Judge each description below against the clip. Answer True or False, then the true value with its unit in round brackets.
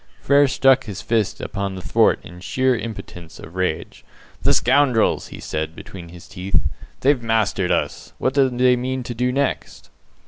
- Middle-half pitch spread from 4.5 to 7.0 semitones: True (5.6 semitones)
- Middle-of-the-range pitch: False (115 Hz)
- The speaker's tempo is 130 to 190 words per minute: True (170 wpm)